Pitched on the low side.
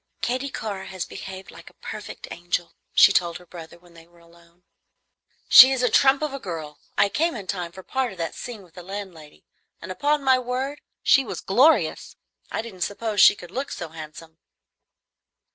No: high, 190 Hz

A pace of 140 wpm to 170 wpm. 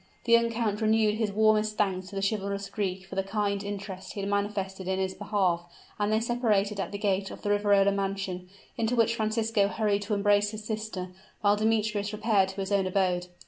No: fast, 205 wpm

